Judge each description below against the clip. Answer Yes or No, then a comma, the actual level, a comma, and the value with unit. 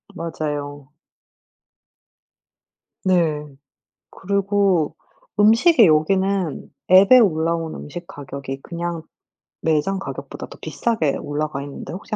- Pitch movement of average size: Yes, average, 4.6 semitones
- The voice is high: No, medium, 170 Hz